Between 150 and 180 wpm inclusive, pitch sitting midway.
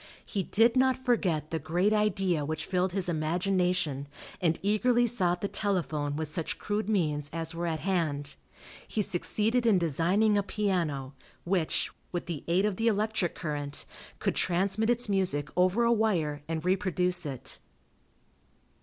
Yes: average, 155 wpm; medium, 180 Hz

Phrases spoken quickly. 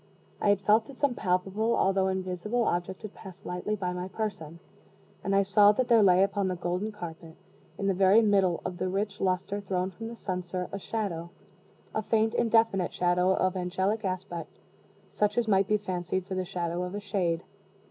No: average, 190 wpm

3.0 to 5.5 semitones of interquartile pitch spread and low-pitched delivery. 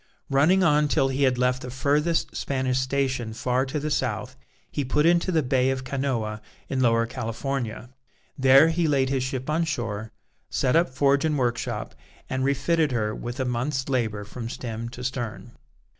No: narrow, 2.5 semitones; low, 130 Hz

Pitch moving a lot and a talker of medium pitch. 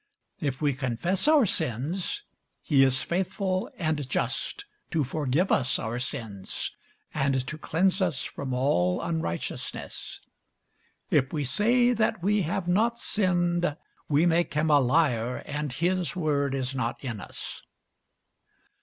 Yes: wide, 5.7 semitones; medium, 150 Hz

